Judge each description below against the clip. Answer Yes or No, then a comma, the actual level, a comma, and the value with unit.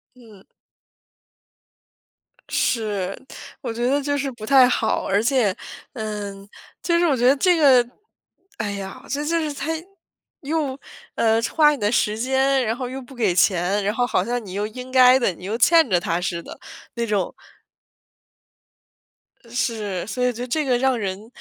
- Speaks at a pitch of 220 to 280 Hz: Yes, high, 240 Hz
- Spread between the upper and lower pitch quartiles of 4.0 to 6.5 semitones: Yes, average, 4.4 semitones